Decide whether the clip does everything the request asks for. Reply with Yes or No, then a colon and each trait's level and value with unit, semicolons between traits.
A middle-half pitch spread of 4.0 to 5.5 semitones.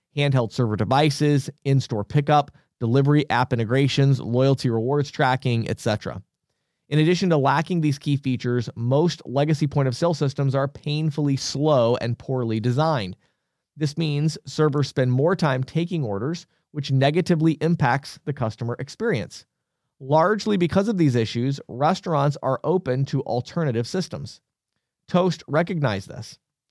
No: average, 3.5 semitones